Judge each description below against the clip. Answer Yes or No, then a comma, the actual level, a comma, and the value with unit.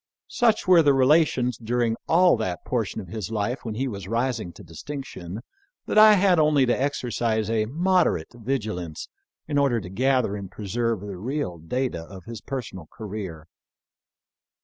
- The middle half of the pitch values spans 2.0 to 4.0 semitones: No, wide, 5.5 semitones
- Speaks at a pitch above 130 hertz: No, low, 115 Hz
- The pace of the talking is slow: No, average, 165 wpm